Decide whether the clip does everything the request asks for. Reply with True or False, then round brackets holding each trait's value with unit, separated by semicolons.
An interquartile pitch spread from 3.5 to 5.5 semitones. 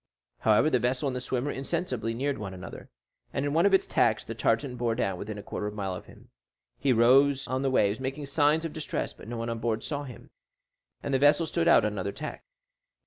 True (4.4 semitones)